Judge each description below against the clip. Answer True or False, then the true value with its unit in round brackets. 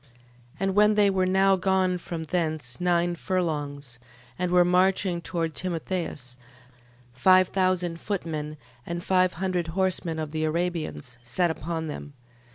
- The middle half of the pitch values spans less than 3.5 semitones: True (2.8 semitones)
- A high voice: False (175 Hz)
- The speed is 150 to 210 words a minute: False (140 wpm)